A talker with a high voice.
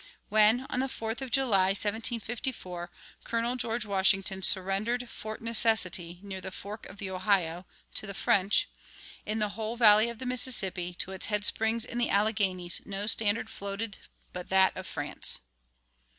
Yes: high, 210 Hz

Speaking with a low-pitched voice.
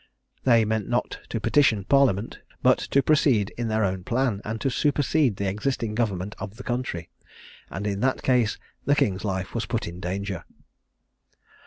Yes: low, 110 Hz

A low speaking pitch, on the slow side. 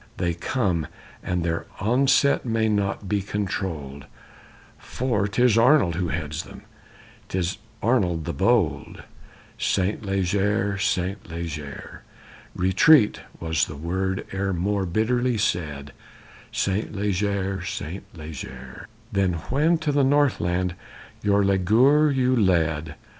Yes: very low, 95 Hz; slow, 115 wpm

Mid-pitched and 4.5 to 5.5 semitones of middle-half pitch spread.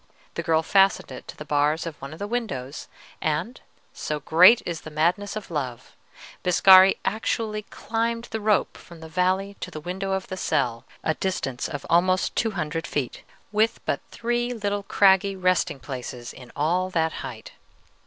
Yes: medium, 180 Hz; average, 4.8 semitones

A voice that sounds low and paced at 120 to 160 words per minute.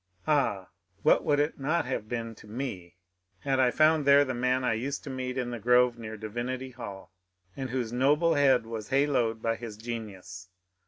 No: low, 125 Hz; average, 190 wpm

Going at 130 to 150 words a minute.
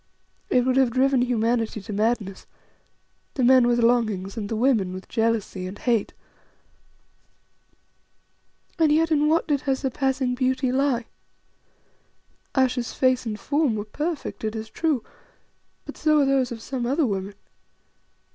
Yes: average, 145 wpm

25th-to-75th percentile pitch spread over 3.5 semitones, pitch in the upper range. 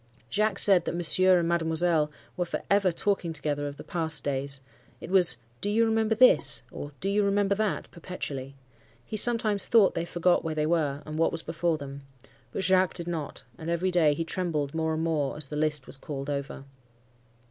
No: average, 4.1 semitones; medium, 165 Hz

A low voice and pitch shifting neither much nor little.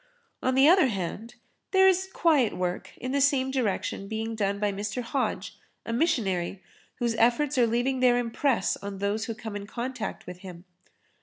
No: high, 230 Hz; average, 4.6 semitones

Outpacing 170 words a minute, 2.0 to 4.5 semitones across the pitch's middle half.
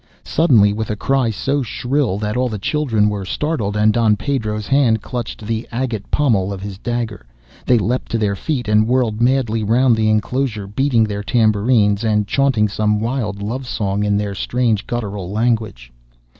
Yes: average, 180 wpm; average, 3.1 semitones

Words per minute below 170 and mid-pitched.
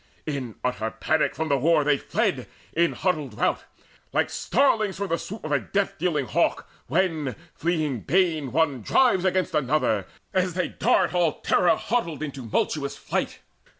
Yes: average, 160 wpm; medium, 155 Hz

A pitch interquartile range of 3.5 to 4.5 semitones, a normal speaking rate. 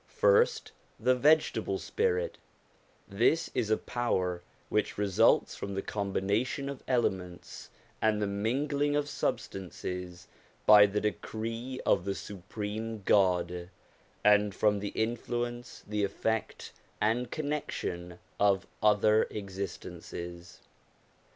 No: average, 3.8 semitones; slow, 105 wpm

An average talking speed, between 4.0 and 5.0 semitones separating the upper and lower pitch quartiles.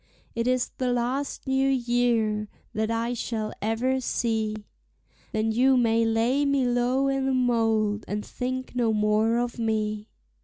No: average, 150 wpm; narrow, 2.6 semitones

